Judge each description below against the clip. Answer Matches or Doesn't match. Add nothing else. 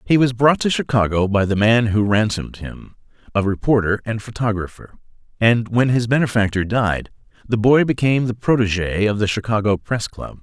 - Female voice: Doesn't match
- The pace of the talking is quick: Doesn't match